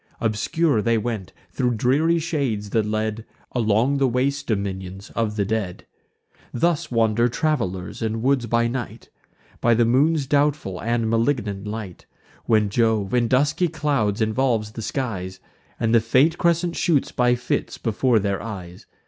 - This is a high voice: No, low, 115 Hz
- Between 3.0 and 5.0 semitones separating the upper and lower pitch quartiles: Yes, average, 4.1 semitones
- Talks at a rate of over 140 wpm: Yes, average, 150 wpm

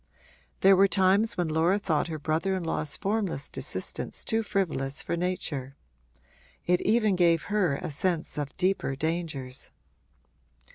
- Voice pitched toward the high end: No, medium, 175 Hz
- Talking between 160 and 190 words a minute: No, average, 140 wpm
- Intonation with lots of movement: No, average, 4.0 semitones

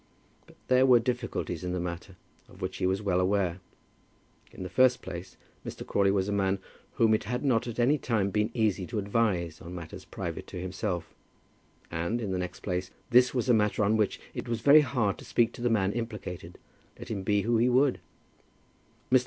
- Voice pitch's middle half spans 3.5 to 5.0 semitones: Yes, average, 4.3 semitones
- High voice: No, low, 105 Hz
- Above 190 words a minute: Yes, fast, 205 wpm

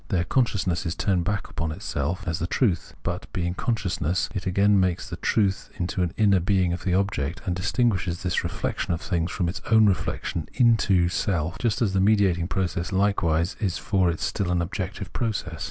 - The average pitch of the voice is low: Yes, very low, 95 Hz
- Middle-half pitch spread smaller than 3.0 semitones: Yes, narrow, 2.6 semitones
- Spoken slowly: No, average, 190 wpm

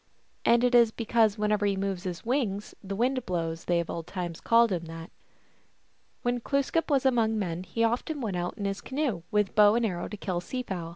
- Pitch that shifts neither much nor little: Yes, average, 4.9 semitones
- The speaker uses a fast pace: Yes, fast, 215 wpm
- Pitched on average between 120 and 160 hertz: No, high, 210 Hz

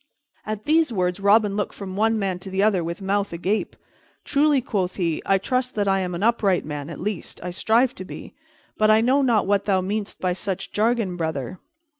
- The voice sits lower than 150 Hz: No, high, 200 Hz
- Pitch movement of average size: Yes, average, 3.1 semitones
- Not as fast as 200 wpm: No, fast, 205 wpm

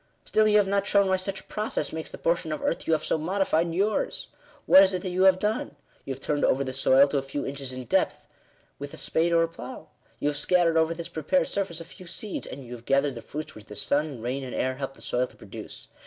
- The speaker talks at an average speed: No, fast, 270 wpm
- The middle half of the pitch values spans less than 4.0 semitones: No, wide, 5.4 semitones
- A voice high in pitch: No, medium, 160 Hz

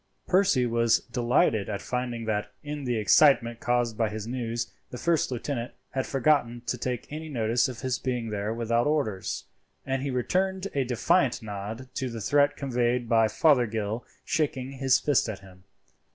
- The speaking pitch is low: Yes, low, 120 Hz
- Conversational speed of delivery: Yes, average, 165 wpm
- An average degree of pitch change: Yes, average, 3.1 semitones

